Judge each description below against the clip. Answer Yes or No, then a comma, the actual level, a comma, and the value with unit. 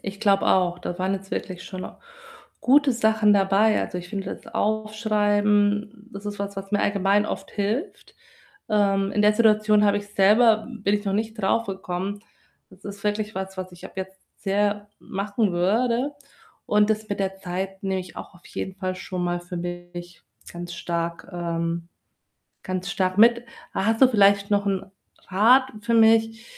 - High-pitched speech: Yes, high, 200 Hz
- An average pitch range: No, narrow, 2.3 semitones